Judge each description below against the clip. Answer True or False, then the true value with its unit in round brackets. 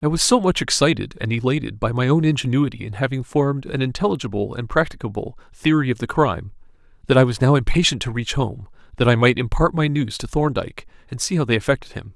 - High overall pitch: False (130 Hz)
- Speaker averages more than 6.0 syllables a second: True (6.4 syllables/s)